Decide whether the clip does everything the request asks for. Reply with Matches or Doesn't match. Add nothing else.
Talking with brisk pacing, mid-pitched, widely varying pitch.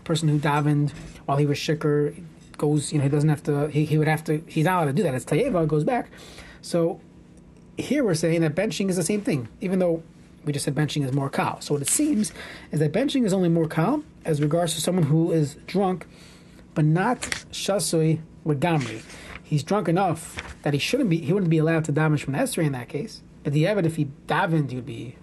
Doesn't match